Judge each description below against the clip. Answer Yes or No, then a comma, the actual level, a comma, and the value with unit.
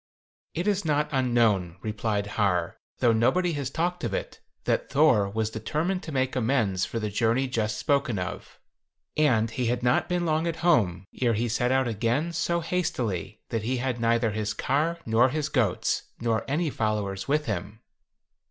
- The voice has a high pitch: No, low, 120 Hz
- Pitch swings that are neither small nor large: No, wide, 5.9 semitones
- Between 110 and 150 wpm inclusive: No, average, 175 wpm